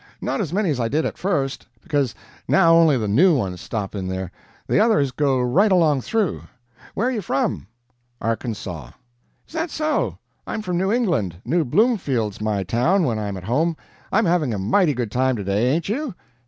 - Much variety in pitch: Yes, wide, 9.0 semitones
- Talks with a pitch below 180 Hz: Yes, medium, 140 Hz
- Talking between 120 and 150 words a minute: No, average, 190 wpm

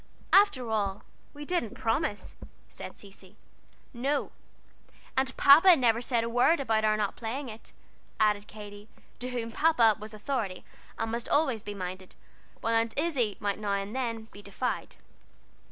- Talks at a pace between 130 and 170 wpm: Yes, average, 155 wpm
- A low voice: No, high, 225 Hz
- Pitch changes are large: No, average, 4.0 semitones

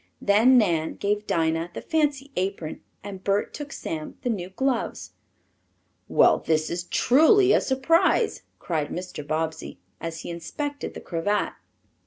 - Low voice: No, high, 200 Hz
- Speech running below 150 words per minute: Yes, average, 140 wpm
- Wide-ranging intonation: Yes, wide, 8.3 semitones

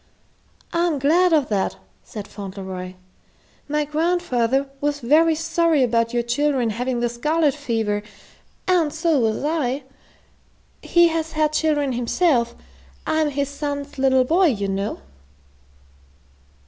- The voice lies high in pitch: Yes, very high, 285 Hz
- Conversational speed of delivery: No, slow, 120 wpm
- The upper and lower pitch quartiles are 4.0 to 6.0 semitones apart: Yes, average, 5.0 semitones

